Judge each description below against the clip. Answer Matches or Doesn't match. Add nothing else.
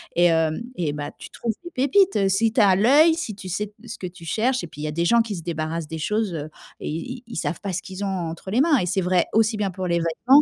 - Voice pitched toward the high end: Matches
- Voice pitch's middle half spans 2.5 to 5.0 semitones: Doesn't match